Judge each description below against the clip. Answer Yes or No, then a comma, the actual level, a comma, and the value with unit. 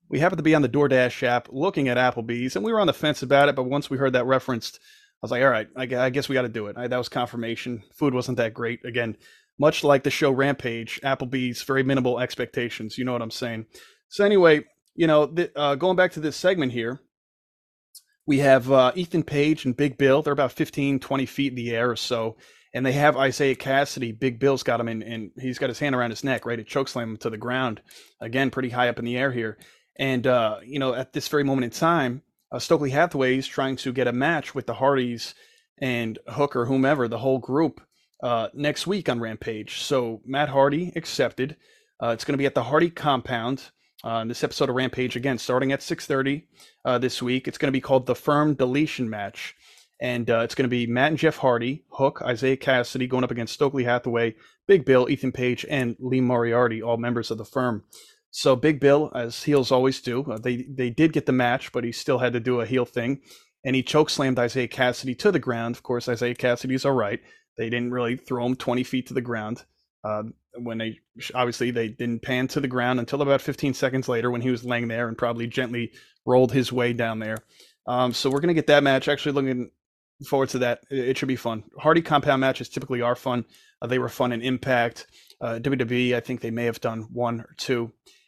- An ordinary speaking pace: No, fast, 230 wpm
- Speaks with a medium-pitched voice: No, low, 130 Hz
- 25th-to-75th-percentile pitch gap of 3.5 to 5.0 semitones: No, narrow, 2.6 semitones